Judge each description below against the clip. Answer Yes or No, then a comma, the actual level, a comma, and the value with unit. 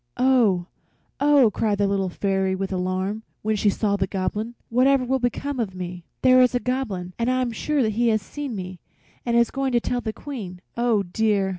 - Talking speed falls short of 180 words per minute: No, average, 200 wpm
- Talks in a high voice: Yes, high, 220 Hz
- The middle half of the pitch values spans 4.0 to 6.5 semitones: Yes, average, 4.7 semitones